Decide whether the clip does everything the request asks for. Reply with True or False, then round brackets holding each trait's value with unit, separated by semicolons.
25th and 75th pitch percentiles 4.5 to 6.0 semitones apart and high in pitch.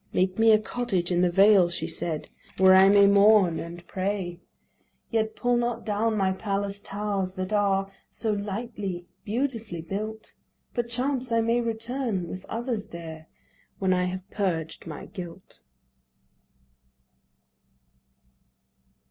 False (3.4 semitones; 200 Hz)